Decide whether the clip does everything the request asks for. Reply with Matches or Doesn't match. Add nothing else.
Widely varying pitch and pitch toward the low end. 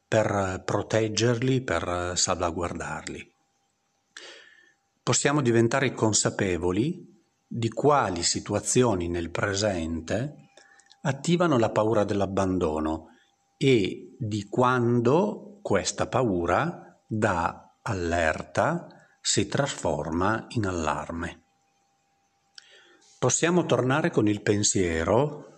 Matches